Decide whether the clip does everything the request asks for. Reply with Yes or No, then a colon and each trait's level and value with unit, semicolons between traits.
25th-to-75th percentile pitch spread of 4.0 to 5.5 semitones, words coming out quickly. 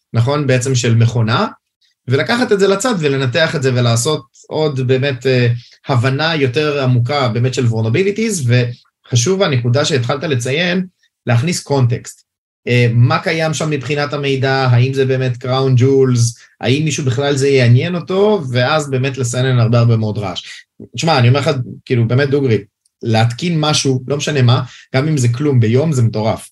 No: average, 3.4 semitones; fast, 160 wpm